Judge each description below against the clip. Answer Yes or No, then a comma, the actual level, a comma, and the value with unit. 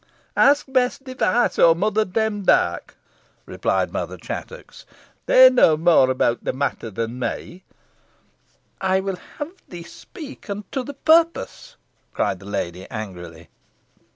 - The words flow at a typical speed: No, slow, 125 wpm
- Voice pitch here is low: No, high, 190 Hz